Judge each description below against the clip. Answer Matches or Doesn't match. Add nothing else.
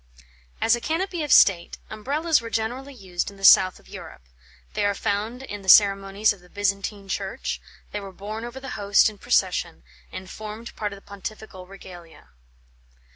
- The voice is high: Matches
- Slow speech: Doesn't match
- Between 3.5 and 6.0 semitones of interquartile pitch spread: Doesn't match